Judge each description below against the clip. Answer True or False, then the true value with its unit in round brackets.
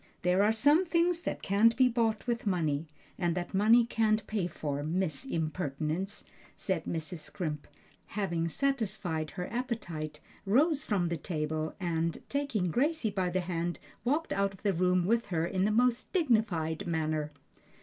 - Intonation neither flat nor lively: False (5.8 semitones)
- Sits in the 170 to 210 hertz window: True (190 Hz)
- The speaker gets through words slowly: False (160 wpm)